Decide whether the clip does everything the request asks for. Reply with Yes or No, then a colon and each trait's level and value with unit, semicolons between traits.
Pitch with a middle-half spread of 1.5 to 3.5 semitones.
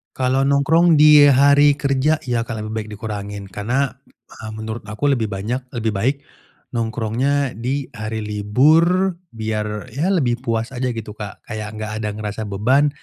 No: average, 4.6 semitones